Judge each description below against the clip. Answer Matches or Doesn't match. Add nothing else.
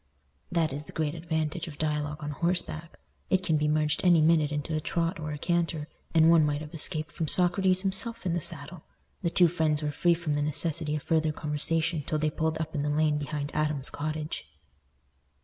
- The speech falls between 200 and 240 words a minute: Matches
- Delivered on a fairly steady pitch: Matches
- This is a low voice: Doesn't match